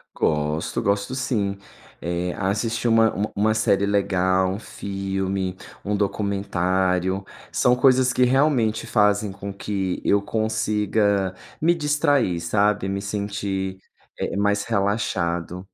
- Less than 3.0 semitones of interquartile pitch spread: Yes, narrow, 2.5 semitones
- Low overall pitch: Yes, low, 100 Hz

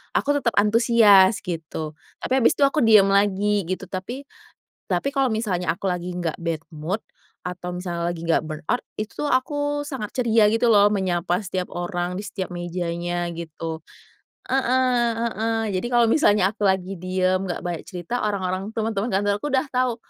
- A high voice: Yes, high, 195 Hz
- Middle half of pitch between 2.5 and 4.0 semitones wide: No, average, 4.6 semitones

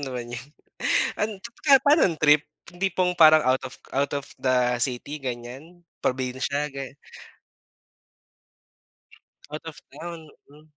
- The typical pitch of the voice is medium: Yes, medium, 145 Hz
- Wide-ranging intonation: No, average, 4.4 semitones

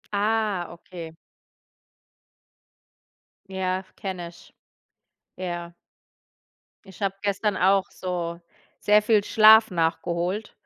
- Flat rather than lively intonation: No, average, 3.1 semitones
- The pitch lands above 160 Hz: Yes, high, 190 Hz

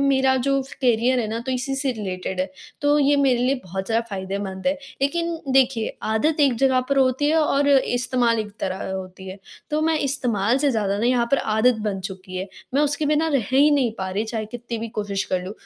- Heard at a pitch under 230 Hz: No, high, 245 Hz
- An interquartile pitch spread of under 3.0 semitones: No, average, 5.2 semitones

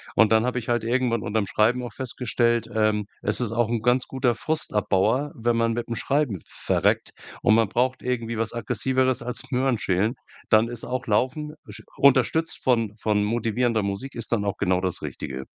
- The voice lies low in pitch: Yes, low, 115 Hz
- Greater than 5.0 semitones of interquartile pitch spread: No, average, 2.7 semitones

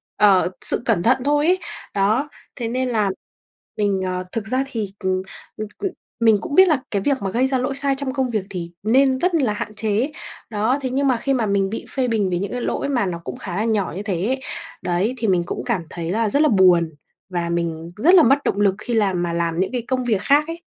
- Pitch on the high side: Yes, high, 220 Hz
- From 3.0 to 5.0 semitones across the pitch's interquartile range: No, wide, 5.6 semitones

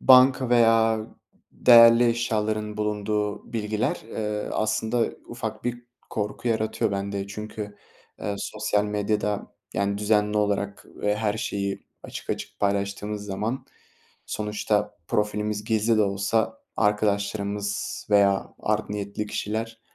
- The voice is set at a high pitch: No, low, 105 Hz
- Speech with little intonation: Yes, narrow, 1.4 semitones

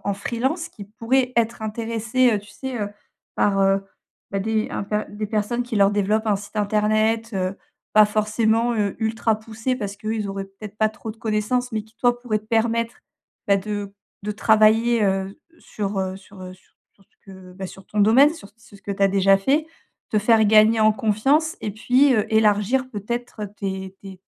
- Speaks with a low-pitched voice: No, high, 215 Hz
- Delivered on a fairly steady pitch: Yes, narrow, 2.3 semitones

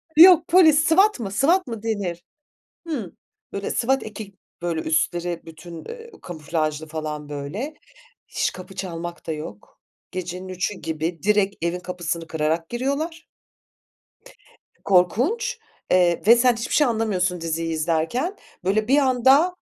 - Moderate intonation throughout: No, wide, 7.6 semitones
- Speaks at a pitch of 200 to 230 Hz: No, medium, 185 Hz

